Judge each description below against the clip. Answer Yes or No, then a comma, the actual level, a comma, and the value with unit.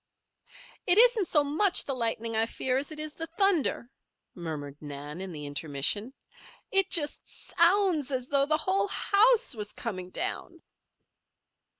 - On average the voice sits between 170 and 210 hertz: No, very high, 275 Hz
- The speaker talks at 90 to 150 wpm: No, average, 160 wpm